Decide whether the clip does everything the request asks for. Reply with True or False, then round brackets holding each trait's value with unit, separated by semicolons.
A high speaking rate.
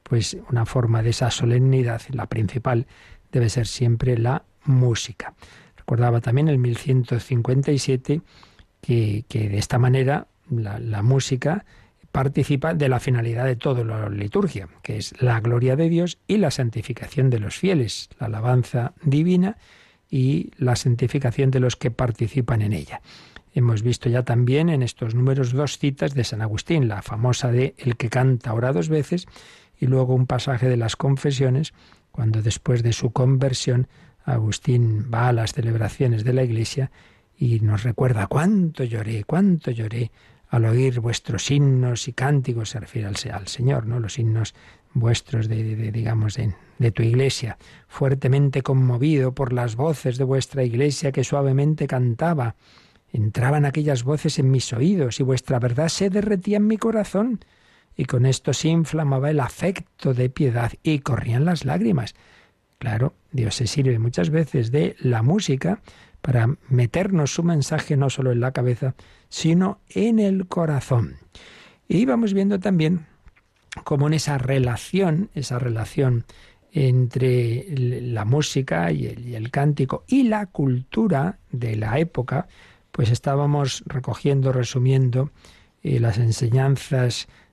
False (150 wpm)